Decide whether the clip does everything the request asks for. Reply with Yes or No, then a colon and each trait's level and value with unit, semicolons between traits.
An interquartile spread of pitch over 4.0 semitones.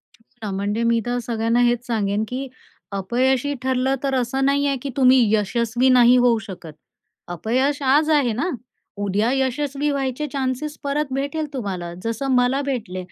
No: average, 3.2 semitones